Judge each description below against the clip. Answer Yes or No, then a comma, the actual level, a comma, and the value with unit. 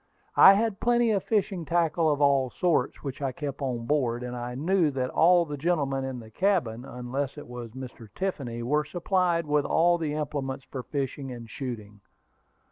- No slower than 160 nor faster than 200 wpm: Yes, average, 185 wpm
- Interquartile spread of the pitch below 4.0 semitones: No, average, 5.3 semitones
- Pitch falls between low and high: Yes, medium, 145 Hz